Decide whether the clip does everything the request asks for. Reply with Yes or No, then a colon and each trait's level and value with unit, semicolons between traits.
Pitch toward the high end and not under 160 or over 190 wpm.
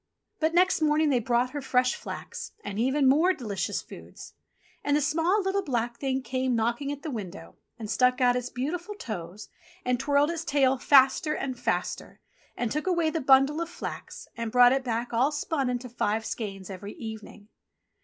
Yes: very high, 260 Hz; average, 185 wpm